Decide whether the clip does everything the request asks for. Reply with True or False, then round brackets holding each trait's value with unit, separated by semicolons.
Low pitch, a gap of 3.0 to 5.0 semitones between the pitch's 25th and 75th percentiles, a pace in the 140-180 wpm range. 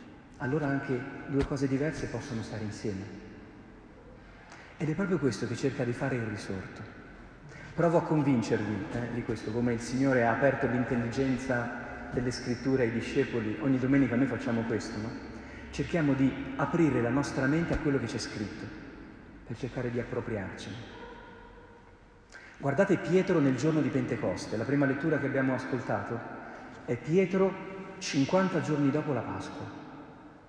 True (130 Hz; 3.5 semitones; 145 wpm)